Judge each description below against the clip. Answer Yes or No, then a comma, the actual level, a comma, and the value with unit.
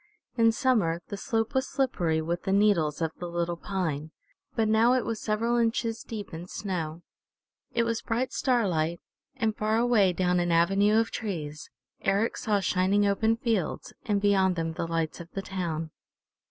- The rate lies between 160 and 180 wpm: Yes, average, 170 wpm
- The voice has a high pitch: Yes, high, 195 Hz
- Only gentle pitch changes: No, average, 4.8 semitones